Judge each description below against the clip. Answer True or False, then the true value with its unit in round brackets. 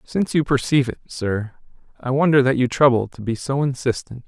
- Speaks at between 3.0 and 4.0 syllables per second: False (5.8 syllables/s)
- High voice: False (130 Hz)